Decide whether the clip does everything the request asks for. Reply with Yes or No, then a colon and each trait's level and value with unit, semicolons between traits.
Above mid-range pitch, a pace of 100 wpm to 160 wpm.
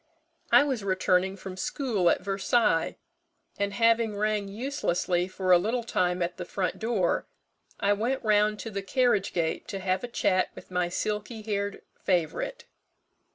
Yes: high, 200 Hz; average, 155 wpm